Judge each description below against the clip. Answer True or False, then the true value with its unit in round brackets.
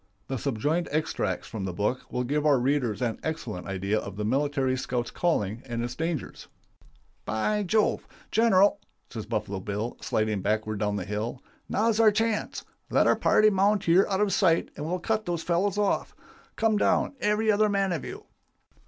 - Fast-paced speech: False (180 wpm)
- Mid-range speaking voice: True (145 Hz)